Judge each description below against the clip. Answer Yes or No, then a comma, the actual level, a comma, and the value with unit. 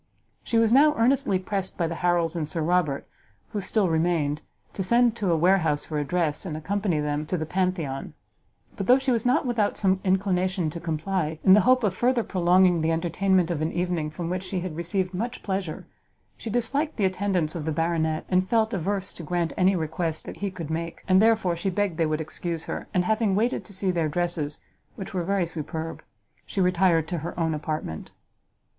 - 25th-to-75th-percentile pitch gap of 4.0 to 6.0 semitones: No, average, 3.4 semitones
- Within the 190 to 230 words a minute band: Yes, fast, 205 wpm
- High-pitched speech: No, medium, 180 Hz